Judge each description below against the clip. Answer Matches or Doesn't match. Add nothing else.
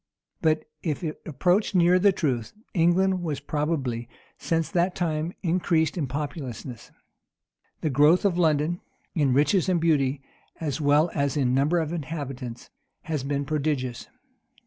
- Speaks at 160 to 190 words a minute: Doesn't match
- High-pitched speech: Doesn't match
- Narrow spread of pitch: Doesn't match